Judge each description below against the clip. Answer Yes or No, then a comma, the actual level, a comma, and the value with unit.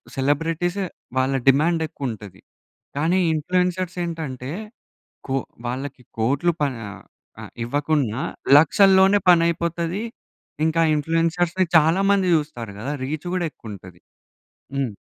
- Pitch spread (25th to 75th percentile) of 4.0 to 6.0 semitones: Yes, average, 4.6 semitones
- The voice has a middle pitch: Yes, medium, 155 Hz